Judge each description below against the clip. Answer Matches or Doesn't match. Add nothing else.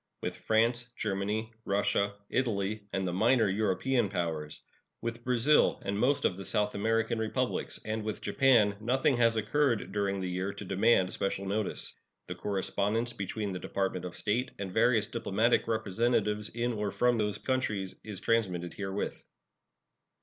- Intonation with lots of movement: Doesn't match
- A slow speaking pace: Doesn't match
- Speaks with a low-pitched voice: Matches